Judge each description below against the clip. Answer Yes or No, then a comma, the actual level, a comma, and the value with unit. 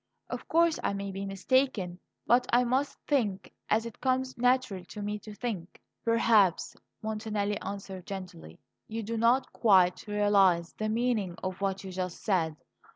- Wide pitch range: No, average, 3.8 semitones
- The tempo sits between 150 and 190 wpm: Yes, average, 155 wpm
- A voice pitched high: Yes, high, 205 Hz